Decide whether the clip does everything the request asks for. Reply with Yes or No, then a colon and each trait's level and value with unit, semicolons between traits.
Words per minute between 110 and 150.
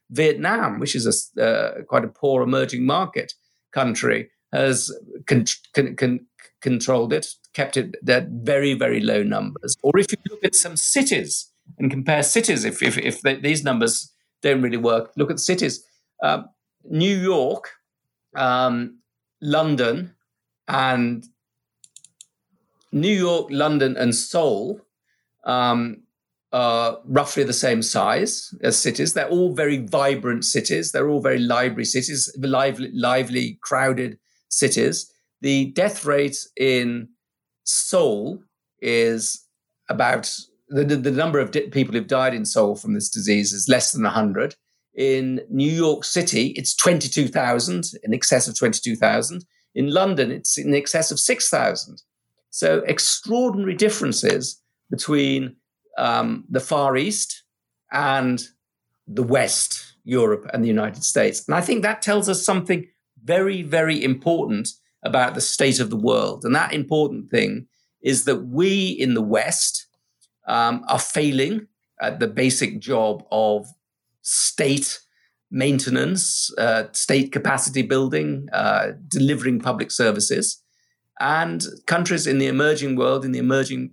Yes: slow, 135 wpm